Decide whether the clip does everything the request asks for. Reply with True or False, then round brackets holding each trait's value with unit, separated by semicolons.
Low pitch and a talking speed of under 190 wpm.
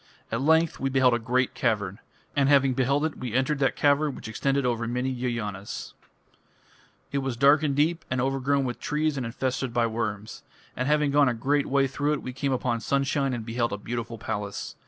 False (130 Hz; 200 wpm)